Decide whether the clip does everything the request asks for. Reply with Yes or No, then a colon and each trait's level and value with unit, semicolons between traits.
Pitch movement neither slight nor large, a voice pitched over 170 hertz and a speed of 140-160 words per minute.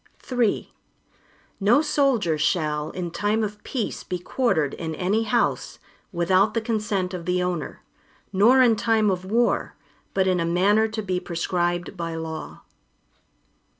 Yes: average, 4.1 semitones; high, 190 Hz; average, 145 wpm